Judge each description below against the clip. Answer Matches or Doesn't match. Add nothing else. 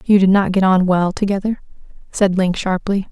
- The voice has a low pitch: Doesn't match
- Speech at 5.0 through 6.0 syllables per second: Matches